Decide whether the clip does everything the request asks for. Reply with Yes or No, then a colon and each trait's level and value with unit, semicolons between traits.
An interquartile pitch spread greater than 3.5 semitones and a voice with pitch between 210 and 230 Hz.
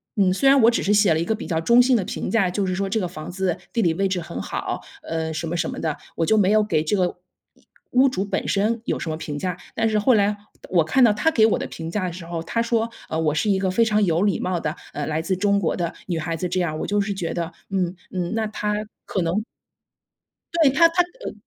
No: average, 4.2 semitones; high, 190 Hz